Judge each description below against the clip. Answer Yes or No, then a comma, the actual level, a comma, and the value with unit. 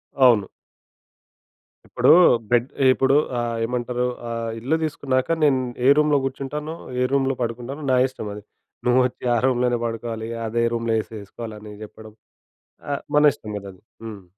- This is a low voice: Yes, low, 120 Hz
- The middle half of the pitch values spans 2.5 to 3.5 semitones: Yes, average, 2.9 semitones